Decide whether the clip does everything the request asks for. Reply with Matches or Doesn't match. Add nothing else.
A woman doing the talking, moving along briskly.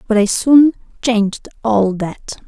Doesn't match